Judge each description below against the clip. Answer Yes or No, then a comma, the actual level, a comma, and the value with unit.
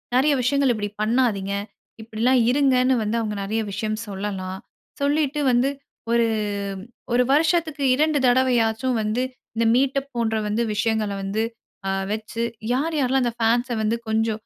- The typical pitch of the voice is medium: No, high, 235 Hz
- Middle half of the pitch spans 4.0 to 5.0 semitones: No, average, 3.5 semitones